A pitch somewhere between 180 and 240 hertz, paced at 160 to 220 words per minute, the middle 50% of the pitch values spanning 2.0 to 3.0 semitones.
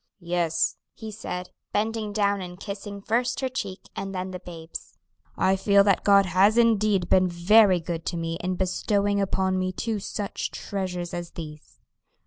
Yes: high, 190 Hz; average, 165 wpm; narrow, 2.5 semitones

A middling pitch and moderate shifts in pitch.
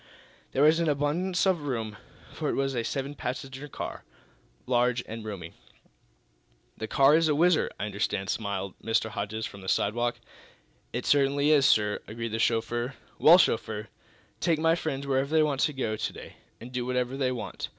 No: low, 130 Hz; average, 4.7 semitones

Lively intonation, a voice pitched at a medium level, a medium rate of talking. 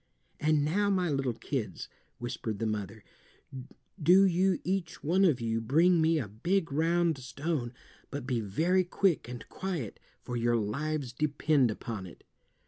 Yes: wide, 6.5 semitones; medium, 145 Hz; average, 150 wpm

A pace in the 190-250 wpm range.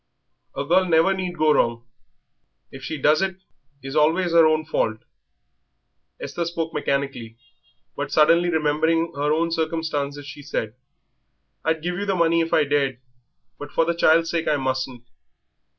No: average, 155 wpm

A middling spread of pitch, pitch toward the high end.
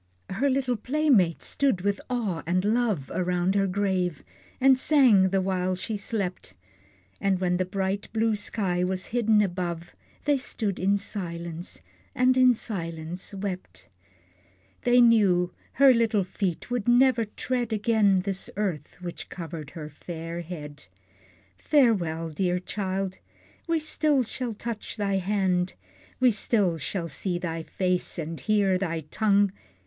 Yes: average, 4.1 semitones; high, 195 Hz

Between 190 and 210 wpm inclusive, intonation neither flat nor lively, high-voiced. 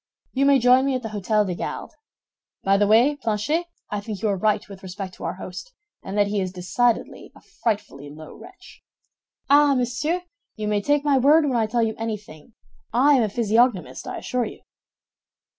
Yes: average, 195 wpm; average, 4.4 semitones; high, 220 Hz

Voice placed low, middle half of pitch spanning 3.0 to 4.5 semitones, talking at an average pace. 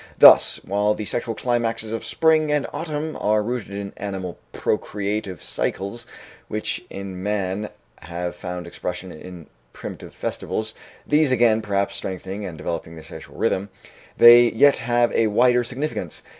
Yes: low, 105 Hz; average, 4.2 semitones; average, 145 wpm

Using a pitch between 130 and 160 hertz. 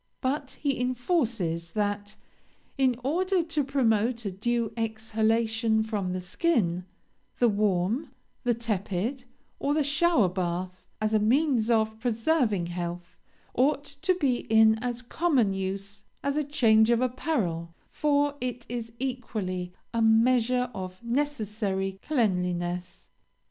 No: high, 225 Hz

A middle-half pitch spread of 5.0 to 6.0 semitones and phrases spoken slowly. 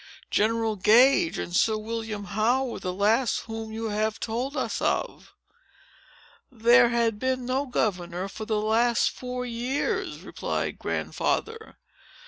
No: average, 2.7 semitones; slow, 130 wpm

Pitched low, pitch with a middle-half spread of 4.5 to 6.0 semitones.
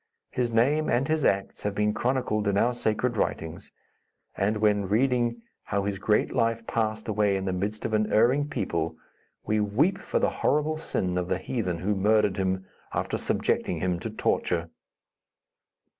No: low, 105 Hz; average, 3.5 semitones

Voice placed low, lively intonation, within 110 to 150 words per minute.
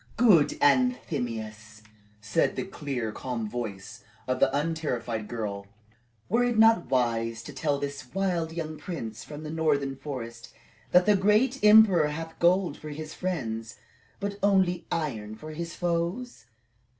No: medium, 150 Hz; wide, 7.4 semitones; average, 140 wpm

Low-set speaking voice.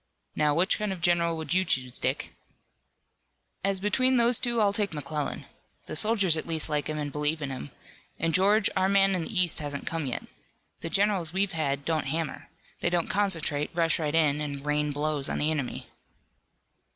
No: medium, 165 Hz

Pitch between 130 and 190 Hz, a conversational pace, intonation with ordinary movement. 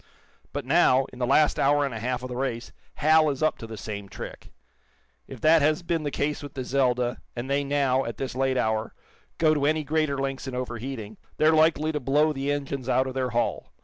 No: low, 135 Hz; fast, 225 wpm; average, 3.0 semitones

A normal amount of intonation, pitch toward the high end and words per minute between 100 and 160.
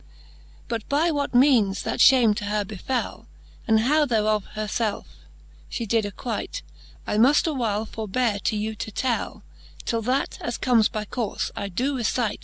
No: average, 3.1 semitones; high, 225 Hz; average, 170 wpm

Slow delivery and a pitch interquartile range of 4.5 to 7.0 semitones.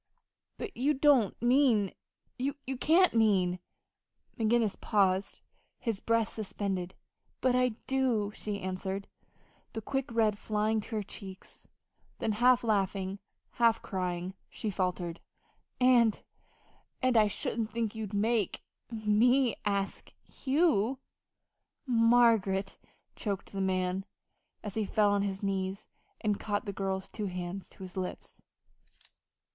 No: slow, 125 wpm; average, 3.3 semitones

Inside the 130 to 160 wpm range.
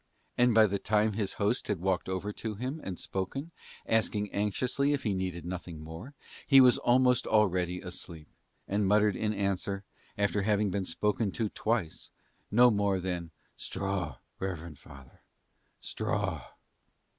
Yes: average, 145 wpm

